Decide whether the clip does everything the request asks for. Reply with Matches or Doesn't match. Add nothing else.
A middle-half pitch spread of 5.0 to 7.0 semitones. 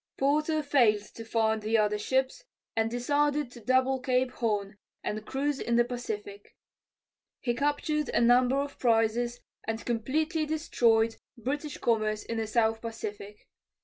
Doesn't match